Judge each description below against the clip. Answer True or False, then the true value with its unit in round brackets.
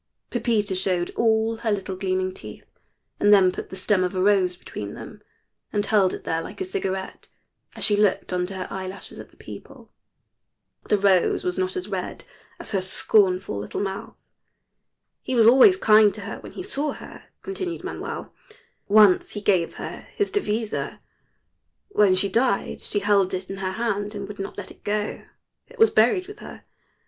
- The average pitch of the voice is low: False (200 Hz)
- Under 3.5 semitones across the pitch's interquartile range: True (2.8 semitones)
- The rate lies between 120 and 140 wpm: False (180 wpm)